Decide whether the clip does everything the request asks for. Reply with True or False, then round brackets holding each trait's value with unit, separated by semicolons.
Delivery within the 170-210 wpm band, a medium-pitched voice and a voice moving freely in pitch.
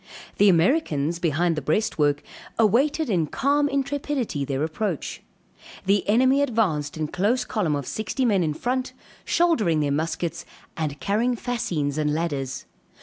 False (140 wpm; 180 Hz; 8.4 semitones)